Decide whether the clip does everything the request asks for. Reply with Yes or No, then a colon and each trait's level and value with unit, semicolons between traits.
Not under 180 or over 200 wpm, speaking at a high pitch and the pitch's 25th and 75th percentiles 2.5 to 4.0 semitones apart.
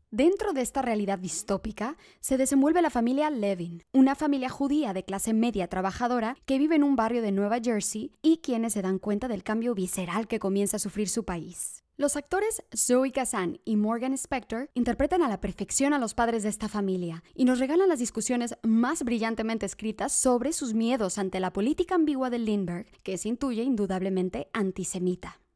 No: average, 185 wpm; high, 230 Hz; average, 5.1 semitones